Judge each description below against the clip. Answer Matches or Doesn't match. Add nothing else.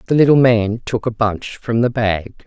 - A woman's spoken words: Matches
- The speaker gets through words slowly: Doesn't match